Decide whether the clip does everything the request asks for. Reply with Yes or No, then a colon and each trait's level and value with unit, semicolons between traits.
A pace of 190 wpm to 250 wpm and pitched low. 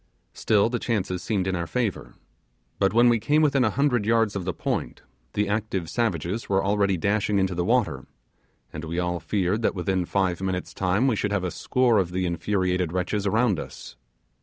Yes: average, 195 wpm; low, 100 Hz